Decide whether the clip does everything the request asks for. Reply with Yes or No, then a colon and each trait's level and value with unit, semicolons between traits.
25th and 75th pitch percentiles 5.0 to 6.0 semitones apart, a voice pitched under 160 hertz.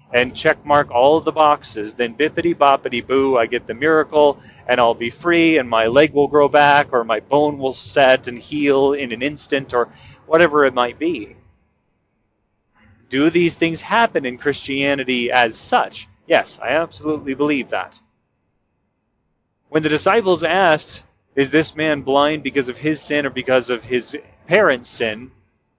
No: average, 3.6 semitones; medium, 140 Hz